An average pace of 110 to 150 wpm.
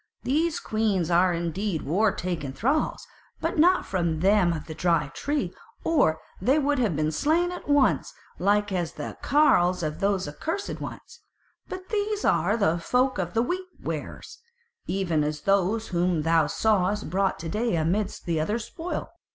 No: average, 165 wpm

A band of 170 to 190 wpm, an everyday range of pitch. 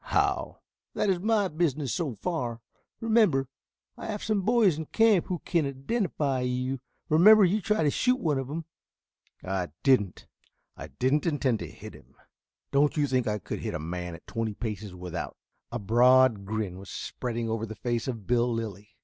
No: average, 185 wpm; wide, 7.5 semitones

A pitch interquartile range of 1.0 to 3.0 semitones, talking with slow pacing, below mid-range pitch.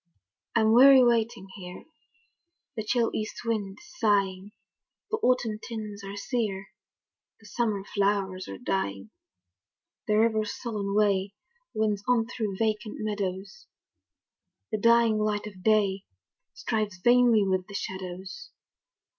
No: average, 2.7 semitones; slow, 120 wpm; high, 210 Hz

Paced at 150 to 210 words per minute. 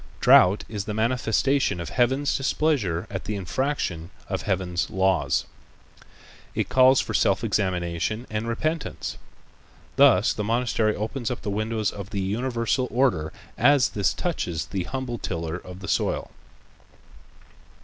No: slow, 135 wpm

